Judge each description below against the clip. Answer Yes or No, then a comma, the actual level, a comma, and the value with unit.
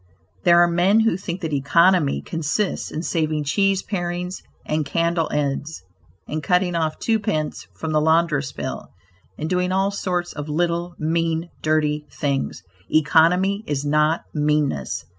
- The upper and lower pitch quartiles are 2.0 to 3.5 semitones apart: Yes, average, 2.8 semitones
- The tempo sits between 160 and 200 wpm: No, average, 145 wpm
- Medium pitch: Yes, medium, 165 Hz